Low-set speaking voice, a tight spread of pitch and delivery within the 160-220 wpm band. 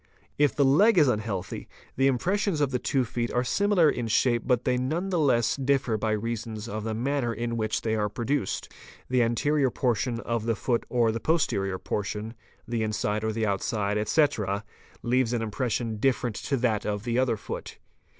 No: low, 120 Hz; average, 3.6 semitones; average, 190 wpm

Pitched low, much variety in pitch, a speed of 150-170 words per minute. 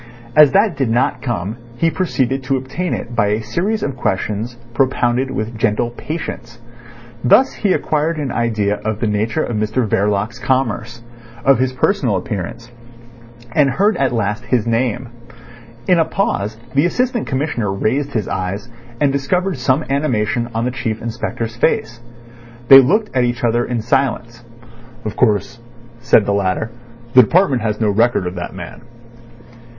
No: low, 120 Hz; average, 3.9 semitones; average, 160 wpm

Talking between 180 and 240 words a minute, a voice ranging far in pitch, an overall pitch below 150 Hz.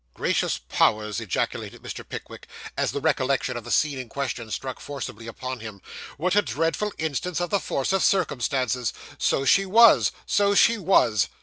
No: average, 170 wpm; wide, 7.2 semitones; medium, 140 Hz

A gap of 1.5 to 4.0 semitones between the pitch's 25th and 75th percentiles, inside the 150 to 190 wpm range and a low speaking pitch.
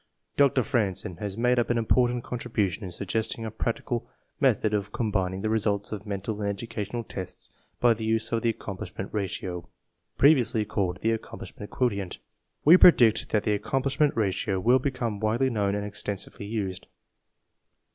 Yes: average, 2.9 semitones; average, 160 wpm; low, 110 Hz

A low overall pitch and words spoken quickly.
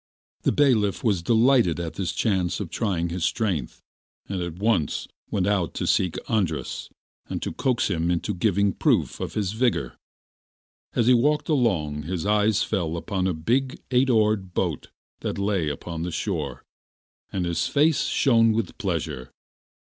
No: low, 100 Hz; average, 160 wpm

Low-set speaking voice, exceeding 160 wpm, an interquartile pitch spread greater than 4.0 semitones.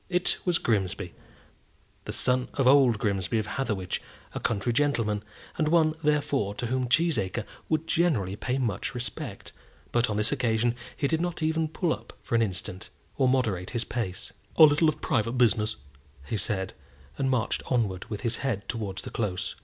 Yes: low, 120 Hz; average, 175 wpm; average, 5.3 semitones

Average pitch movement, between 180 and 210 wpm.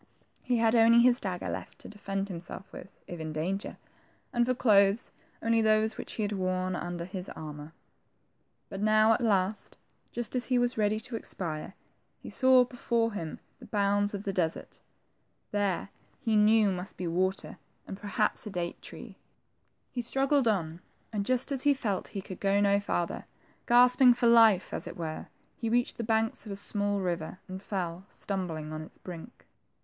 Yes: average, 3.8 semitones; average, 185 wpm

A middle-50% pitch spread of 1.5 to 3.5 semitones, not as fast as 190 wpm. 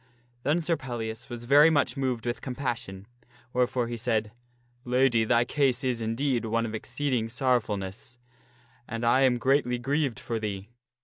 Yes: average, 2.7 semitones; average, 160 wpm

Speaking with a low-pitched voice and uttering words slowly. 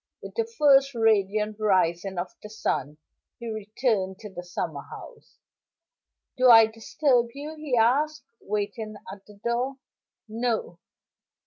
No: high, 220 Hz; slow, 130 wpm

